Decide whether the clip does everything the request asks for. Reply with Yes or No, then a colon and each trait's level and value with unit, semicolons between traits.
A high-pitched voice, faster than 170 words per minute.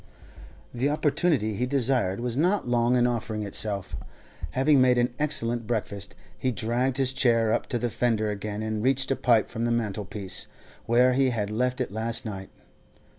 No: low, 120 Hz; average, 180 wpm